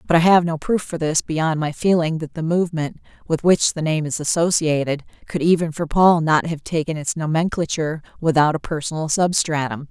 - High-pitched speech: No, medium, 160 Hz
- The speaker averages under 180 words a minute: No, average, 195 wpm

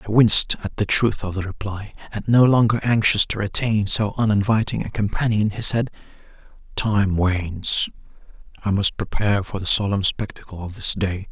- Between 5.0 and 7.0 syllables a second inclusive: Yes, 5.2 syllables/s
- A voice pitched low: Yes, low, 105 Hz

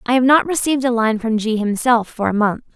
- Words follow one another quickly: Yes, fast, 260 wpm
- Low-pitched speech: No, high, 235 Hz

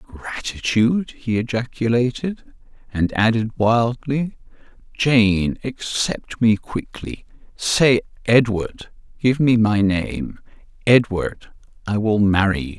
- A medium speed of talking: No, slow, 80 wpm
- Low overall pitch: Yes, low, 110 Hz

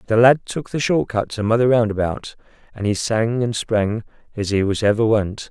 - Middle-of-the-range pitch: No, low, 110 Hz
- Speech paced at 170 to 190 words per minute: No, fast, 205 wpm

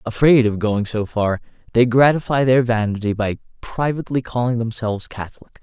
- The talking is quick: No, average, 150 wpm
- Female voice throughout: No, male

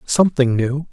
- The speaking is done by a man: Yes, male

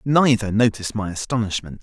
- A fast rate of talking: No, slow, 130 wpm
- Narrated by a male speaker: Yes, male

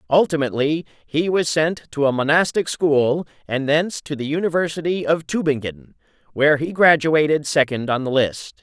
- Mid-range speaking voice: Yes, medium, 150 Hz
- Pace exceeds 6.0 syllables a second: No, 5.1 syllables/s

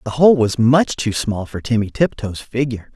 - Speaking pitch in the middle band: No, low, 120 Hz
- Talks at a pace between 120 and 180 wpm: No, fast, 205 wpm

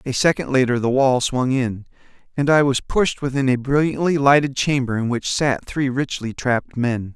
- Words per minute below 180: No, average, 195 wpm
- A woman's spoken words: No, male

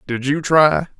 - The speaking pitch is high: No, medium, 140 Hz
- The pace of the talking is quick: No, average, 180 wpm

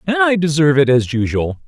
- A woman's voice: No, male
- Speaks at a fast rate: Yes, fast, 215 wpm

